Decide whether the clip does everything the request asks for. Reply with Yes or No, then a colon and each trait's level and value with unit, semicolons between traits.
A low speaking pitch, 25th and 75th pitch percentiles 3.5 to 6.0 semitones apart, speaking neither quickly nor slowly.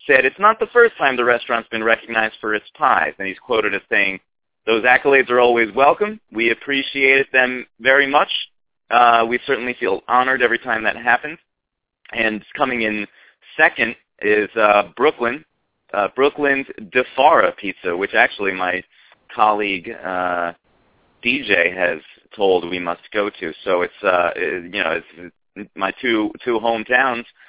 Yes: low, 115 Hz; average, 3.9 semitones; average, 155 wpm